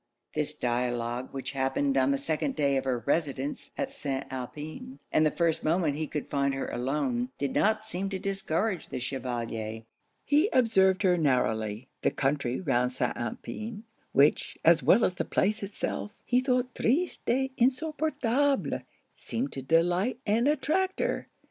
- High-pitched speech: No, medium, 155 Hz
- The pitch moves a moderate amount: No, wide, 8.7 semitones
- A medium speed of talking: Yes, average, 160 wpm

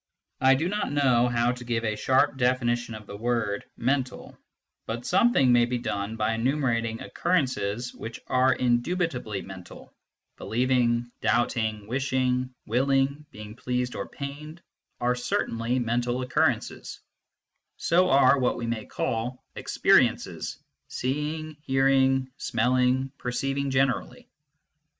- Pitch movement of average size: No, narrow, 2.3 semitones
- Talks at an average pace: No, slow, 125 wpm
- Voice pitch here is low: Yes, low, 125 Hz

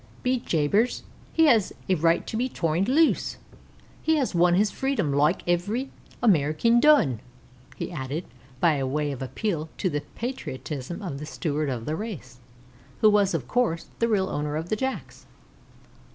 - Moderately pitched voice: Yes, medium, 175 Hz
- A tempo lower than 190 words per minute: Yes, average, 165 wpm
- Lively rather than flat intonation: Yes, wide, 7.5 semitones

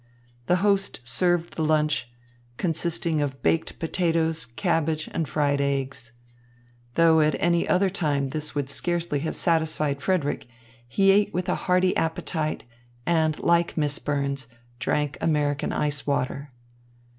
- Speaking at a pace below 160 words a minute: Yes, slow, 135 wpm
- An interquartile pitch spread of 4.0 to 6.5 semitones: No, average, 3.1 semitones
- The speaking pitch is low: No, medium, 155 Hz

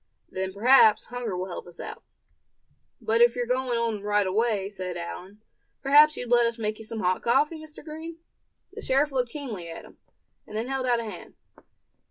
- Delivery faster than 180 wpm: Yes, average, 195 wpm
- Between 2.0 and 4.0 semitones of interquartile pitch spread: No, average, 4.4 semitones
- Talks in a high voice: Yes, high, 230 Hz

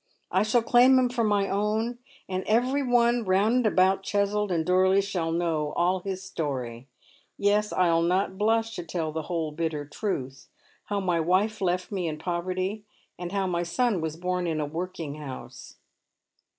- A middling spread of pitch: Yes, average, 4.0 semitones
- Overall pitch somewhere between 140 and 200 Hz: Yes, medium, 185 Hz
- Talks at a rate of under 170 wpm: No, average, 175 wpm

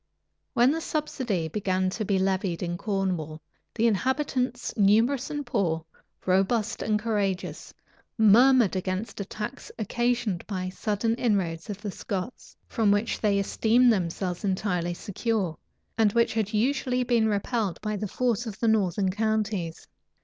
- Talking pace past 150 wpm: No, average, 145 wpm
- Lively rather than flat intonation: No, average, 3.7 semitones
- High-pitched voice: Yes, high, 210 Hz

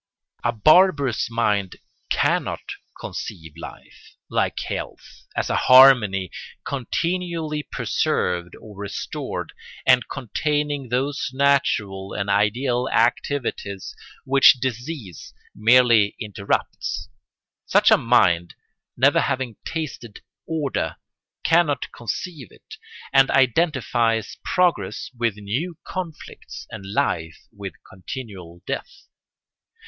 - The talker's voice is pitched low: Yes, low, 120 Hz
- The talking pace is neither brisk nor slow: No, slow, 95 wpm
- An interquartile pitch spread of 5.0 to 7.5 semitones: Yes, wide, 5.6 semitones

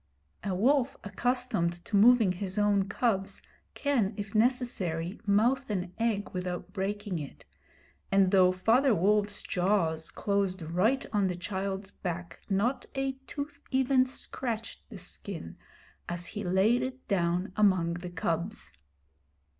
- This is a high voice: Yes, high, 200 Hz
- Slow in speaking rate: Yes, slow, 130 wpm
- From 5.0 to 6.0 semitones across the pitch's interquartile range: No, average, 4.3 semitones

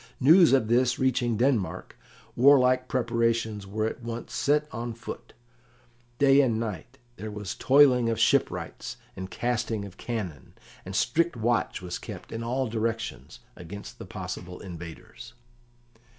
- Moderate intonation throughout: Yes, average, 3.3 semitones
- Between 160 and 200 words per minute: No, slow, 135 wpm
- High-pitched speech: No, low, 115 Hz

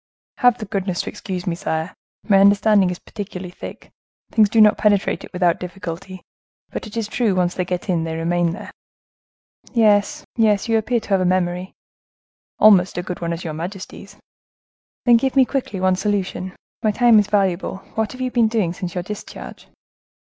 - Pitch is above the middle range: Yes, high, 195 Hz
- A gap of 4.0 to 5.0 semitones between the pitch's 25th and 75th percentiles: No, average, 3.3 semitones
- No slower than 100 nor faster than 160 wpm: No, average, 190 wpm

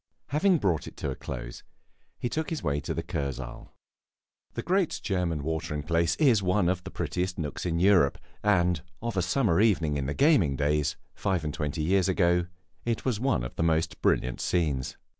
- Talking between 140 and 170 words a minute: No, average, 190 wpm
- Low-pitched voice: Yes, very low, 85 Hz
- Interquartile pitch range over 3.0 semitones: Yes, average, 5.2 semitones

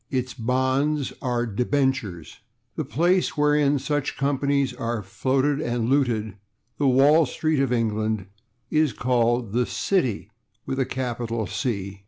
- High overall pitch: No, low, 130 Hz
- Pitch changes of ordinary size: Yes, average, 3.5 semitones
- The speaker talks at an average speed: No, slow, 130 wpm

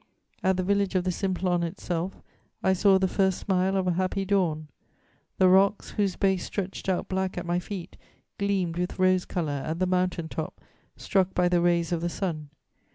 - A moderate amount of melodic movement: No, narrow, 1.7 semitones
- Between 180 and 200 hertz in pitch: Yes, medium, 185 Hz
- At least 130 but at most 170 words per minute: No, average, 190 wpm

